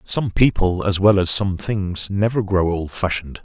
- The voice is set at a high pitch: No, very low, 95 Hz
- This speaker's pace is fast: No, average, 175 wpm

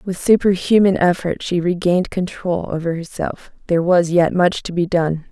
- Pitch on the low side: No, medium, 175 Hz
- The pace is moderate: Yes, average, 160 wpm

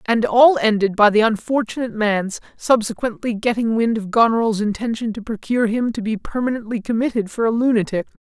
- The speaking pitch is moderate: No, high, 225 Hz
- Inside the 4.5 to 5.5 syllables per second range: No, 5.7 syllables/s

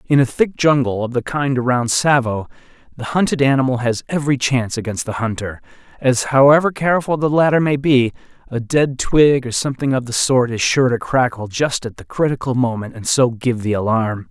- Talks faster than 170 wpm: Yes, average, 195 wpm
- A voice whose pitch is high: No, low, 130 Hz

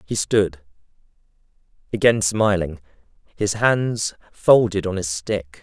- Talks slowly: Yes, slow, 105 wpm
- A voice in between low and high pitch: No, low, 100 Hz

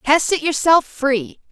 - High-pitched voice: Yes, very high, 290 Hz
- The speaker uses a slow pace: Yes, slow, 120 wpm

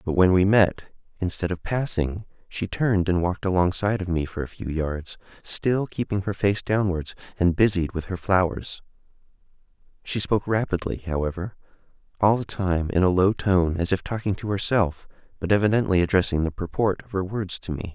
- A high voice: No, very low, 95 Hz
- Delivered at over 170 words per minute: Yes, average, 180 wpm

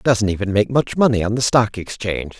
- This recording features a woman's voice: No, male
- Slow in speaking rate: No, fast, 250 wpm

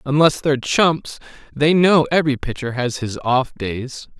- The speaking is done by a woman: No, male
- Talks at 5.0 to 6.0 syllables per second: No, 4.4 syllables/s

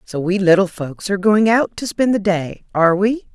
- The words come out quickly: Yes, fast, 235 wpm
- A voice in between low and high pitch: No, high, 195 Hz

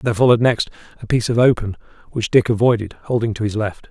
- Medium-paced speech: No, fast, 215 wpm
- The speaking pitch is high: No, low, 110 Hz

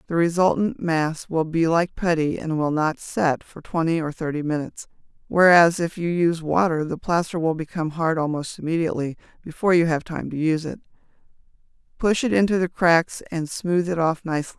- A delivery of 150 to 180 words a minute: No, average, 200 wpm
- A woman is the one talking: Yes, female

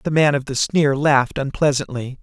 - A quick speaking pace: No, average, 190 wpm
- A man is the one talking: Yes, male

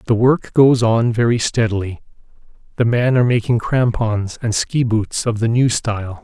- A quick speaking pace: No, average, 165 wpm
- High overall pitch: No, low, 115 Hz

